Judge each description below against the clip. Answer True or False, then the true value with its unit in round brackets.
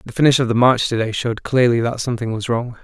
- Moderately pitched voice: False (120 Hz)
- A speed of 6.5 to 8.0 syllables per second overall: True (6.7 syllables/s)